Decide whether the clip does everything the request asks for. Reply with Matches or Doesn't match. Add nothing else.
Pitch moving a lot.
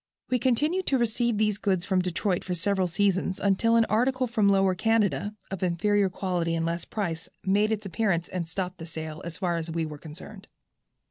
Doesn't match